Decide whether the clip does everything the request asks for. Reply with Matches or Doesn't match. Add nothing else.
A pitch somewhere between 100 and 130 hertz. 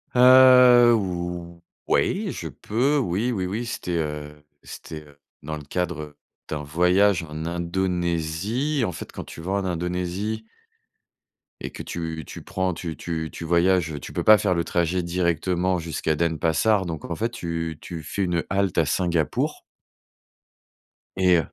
Doesn't match